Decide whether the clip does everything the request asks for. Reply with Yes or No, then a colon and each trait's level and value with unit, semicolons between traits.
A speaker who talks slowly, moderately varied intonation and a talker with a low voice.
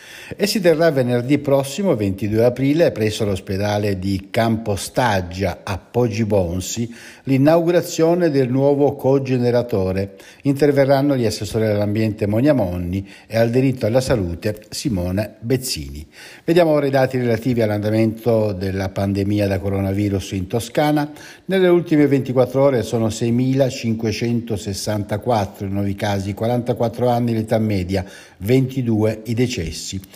Yes: slow, 110 wpm; average, 4.8 semitones; low, 115 Hz